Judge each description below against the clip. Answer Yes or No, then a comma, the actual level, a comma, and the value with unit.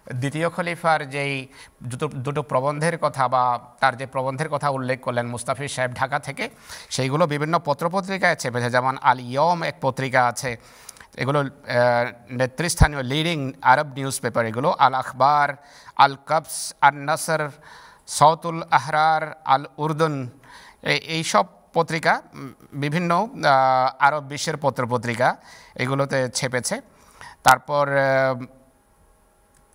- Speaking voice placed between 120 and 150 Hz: Yes, medium, 140 Hz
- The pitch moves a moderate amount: Yes, average, 3.1 semitones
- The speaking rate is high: No, average, 110 wpm